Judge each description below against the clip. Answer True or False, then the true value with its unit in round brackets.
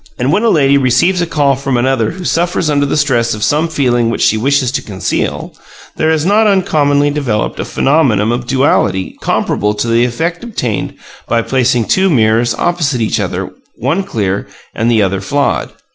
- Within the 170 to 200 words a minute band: True (185 wpm)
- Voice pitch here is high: False (135 Hz)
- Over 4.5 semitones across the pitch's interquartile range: True (5.1 semitones)